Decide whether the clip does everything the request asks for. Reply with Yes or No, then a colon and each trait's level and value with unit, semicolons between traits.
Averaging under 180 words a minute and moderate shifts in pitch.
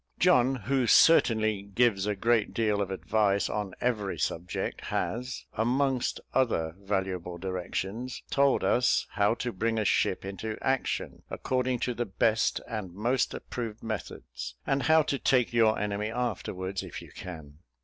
Yes: average, 150 wpm; average, 4.1 semitones